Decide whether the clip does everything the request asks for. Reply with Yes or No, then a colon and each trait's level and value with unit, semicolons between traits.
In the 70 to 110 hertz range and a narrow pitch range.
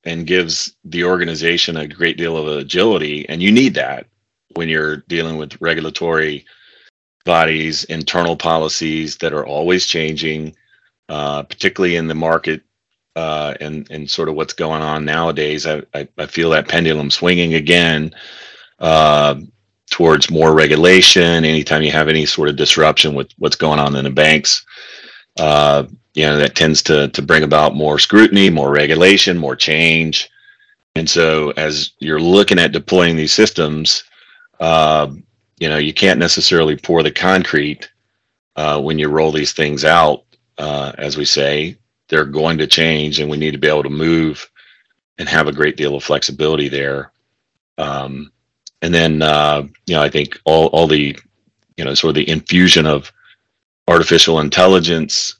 Yes: very low, 80 Hz; narrow, 1.7 semitones